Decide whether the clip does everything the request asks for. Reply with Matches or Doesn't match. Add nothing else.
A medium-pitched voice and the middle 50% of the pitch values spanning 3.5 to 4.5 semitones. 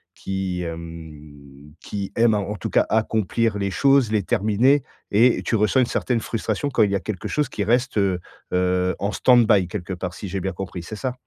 Doesn't match